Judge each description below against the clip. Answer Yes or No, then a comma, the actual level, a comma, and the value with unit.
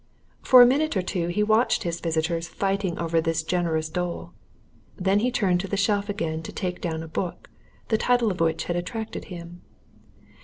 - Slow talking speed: No, average, 190 wpm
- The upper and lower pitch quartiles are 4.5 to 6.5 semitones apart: No, average, 3.6 semitones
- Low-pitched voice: No, medium, 180 Hz